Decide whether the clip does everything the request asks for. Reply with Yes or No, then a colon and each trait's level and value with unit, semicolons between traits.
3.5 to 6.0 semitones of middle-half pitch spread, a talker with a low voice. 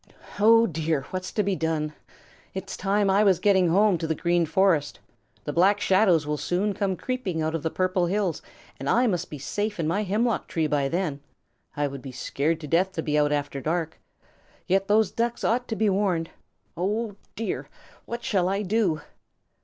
No: average, 4.4 semitones; medium, 185 Hz